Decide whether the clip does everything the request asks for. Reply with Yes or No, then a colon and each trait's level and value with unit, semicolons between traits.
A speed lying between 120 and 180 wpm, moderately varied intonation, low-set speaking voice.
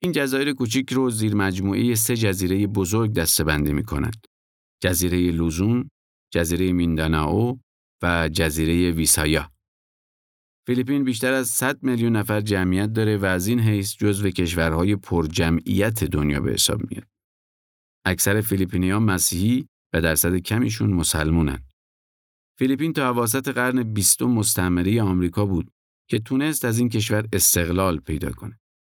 No: average, 135 wpm; wide, 5.7 semitones; low, 100 Hz